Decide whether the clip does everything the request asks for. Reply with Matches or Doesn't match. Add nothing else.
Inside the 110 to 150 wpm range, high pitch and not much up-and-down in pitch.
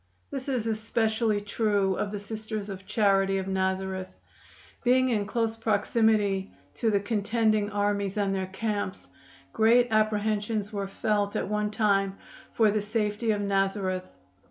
Matches